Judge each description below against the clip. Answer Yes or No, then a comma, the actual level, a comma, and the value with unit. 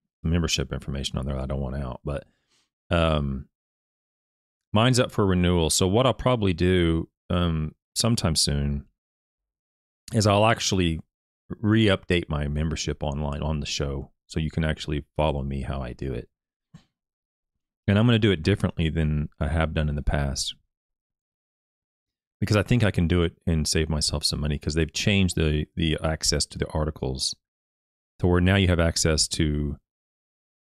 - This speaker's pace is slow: No, average, 170 wpm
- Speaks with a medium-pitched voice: No, very low, 80 Hz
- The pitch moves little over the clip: No, average, 3.9 semitones